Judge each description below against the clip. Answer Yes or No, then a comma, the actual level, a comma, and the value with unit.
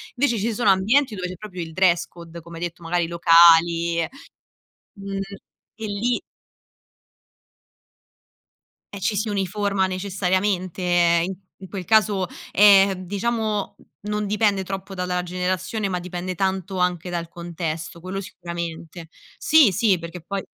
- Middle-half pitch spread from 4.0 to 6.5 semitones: No, average, 2.8 semitones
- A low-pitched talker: No, medium, 185 Hz